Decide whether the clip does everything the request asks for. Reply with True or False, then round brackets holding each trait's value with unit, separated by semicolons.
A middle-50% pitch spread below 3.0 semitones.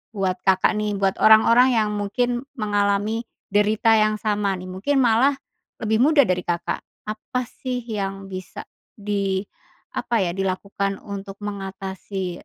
True (2.5 semitones)